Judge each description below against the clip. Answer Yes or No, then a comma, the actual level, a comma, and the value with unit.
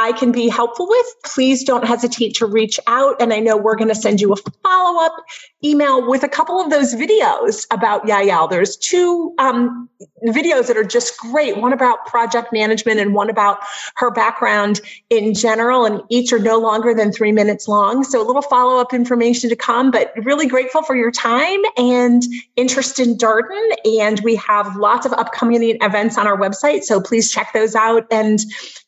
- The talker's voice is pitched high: Yes, high, 235 Hz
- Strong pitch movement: No, average, 3.3 semitones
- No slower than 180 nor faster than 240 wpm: Yes, average, 185 wpm